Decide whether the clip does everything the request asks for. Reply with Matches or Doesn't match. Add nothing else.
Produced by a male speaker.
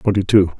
Matches